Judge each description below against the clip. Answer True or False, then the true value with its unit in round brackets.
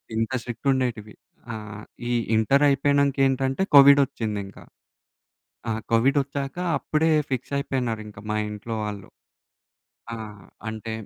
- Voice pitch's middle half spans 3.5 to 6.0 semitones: True (4.1 semitones)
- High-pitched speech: False (125 Hz)